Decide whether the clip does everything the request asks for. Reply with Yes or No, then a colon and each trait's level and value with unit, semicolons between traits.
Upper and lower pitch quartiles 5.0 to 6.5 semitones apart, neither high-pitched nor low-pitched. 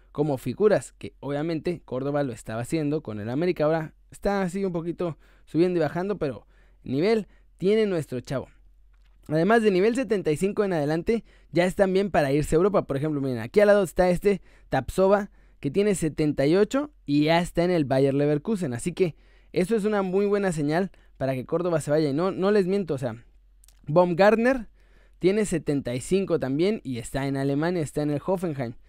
Yes: wide, 5.6 semitones; medium, 165 Hz